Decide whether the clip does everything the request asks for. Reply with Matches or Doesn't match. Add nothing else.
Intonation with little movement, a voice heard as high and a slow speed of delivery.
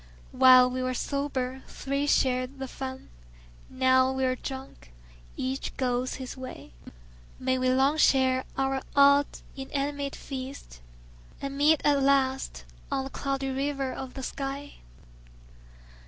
Matches